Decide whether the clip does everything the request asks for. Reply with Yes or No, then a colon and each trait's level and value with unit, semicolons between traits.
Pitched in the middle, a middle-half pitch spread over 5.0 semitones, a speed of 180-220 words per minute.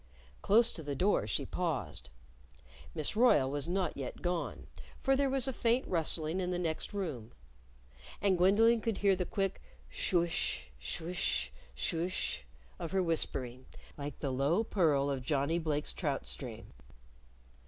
No: medium, 165 Hz; wide, 5.6 semitones; average, 155 wpm